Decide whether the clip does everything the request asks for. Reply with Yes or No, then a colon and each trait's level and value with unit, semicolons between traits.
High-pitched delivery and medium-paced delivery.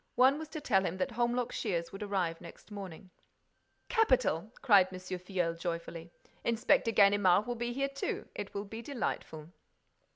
Yes: high, 200 Hz; average, 160 wpm